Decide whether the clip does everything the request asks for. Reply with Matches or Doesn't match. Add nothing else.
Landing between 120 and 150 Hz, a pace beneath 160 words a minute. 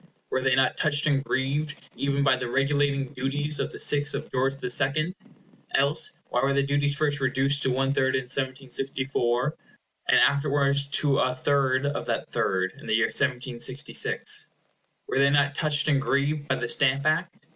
Doesn't match